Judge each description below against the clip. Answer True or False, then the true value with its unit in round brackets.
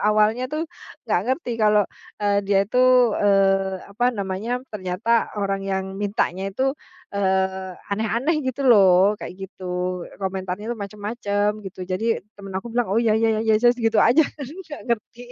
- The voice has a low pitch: False (205 Hz)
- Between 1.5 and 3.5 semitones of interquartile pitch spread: True (3.1 semitones)